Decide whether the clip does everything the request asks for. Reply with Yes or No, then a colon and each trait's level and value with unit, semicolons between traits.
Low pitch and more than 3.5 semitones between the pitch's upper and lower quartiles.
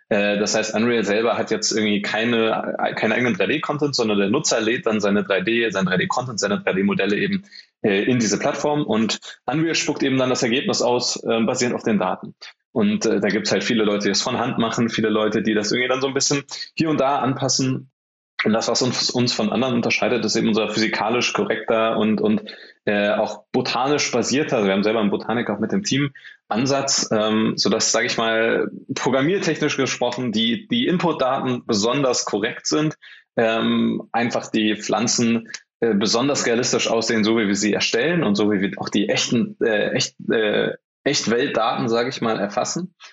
Yes: low, 115 Hz; average, 4.3 semitones